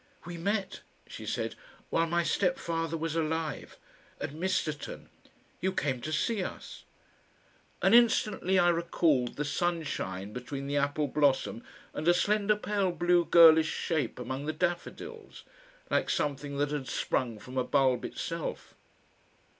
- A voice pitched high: No, medium, 160 Hz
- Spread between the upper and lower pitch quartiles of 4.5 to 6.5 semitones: No, average, 3.7 semitones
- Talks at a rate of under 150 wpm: Yes, average, 140 wpm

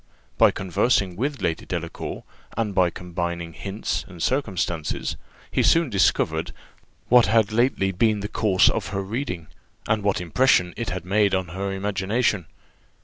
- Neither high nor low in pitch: No, very low, 95 Hz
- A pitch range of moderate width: Yes, average, 3.7 semitones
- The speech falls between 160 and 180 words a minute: No, average, 145 wpm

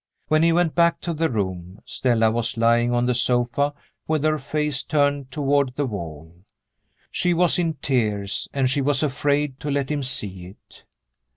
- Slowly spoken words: No, average, 175 wpm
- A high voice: No, low, 135 Hz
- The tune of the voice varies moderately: Yes, average, 4.4 semitones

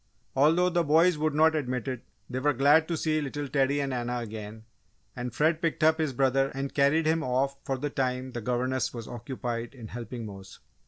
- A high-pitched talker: No, low, 135 Hz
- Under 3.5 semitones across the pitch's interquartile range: No, average, 3.8 semitones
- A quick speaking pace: Yes, fast, 210 wpm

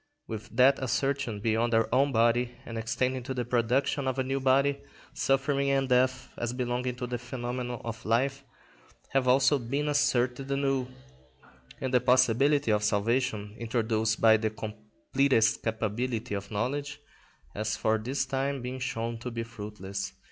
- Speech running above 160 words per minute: No, average, 155 wpm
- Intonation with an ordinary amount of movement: Yes, average, 3.0 semitones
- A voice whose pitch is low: Yes, low, 125 Hz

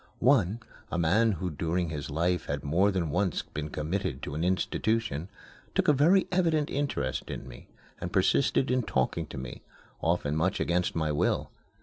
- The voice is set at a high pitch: No, very low, 90 Hz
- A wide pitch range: Yes, wide, 6.6 semitones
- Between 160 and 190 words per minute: Yes, average, 170 wpm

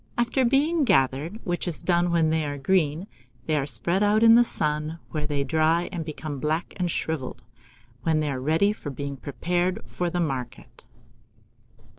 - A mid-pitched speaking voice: Yes, medium, 160 Hz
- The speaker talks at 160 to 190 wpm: Yes, average, 175 wpm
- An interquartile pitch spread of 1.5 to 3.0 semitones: No, average, 3.7 semitones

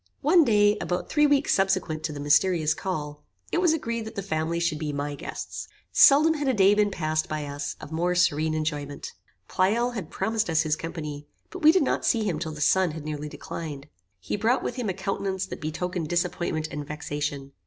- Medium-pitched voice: Yes, medium, 170 Hz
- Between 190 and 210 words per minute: Yes, fast, 205 wpm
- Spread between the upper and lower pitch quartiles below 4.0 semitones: No, wide, 5.5 semitones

